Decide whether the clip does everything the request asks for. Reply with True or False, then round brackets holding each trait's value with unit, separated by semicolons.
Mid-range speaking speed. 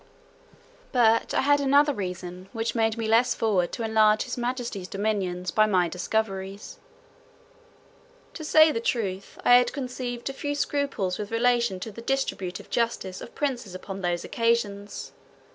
True (150 wpm)